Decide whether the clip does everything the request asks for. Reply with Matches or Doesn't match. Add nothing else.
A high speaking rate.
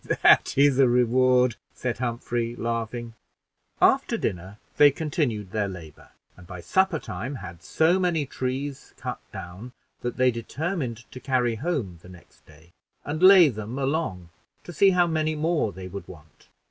Doesn't match